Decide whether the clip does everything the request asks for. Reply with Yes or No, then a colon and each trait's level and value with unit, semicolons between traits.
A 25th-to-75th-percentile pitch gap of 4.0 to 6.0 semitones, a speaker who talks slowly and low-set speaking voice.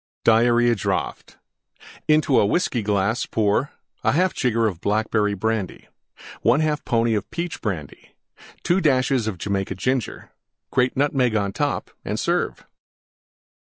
Yes: average, 4.6 semitones; slow, 110 wpm; low, 115 Hz